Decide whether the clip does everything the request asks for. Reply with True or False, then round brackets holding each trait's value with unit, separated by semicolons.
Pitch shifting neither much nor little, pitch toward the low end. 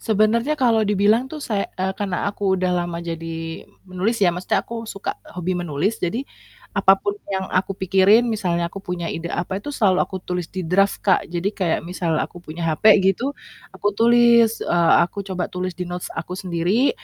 False (3.2 semitones; 190 Hz)